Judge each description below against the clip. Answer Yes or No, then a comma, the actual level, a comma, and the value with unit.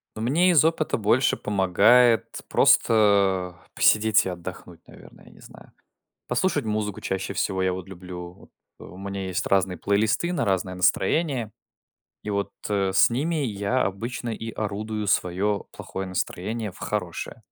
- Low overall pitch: Yes, low, 105 Hz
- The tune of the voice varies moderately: Yes, average, 3.4 semitones